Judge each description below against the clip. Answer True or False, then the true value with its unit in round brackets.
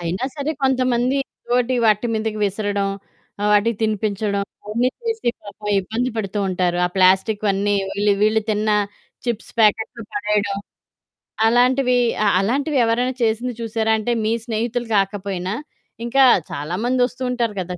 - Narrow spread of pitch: False (3.2 semitones)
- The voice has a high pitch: True (215 Hz)